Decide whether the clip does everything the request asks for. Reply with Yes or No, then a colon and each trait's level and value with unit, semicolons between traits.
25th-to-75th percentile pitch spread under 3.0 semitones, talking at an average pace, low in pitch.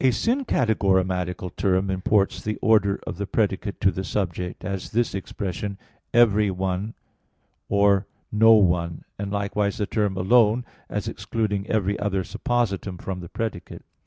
Yes: narrow, 2.4 semitones; average, 145 wpm; low, 100 Hz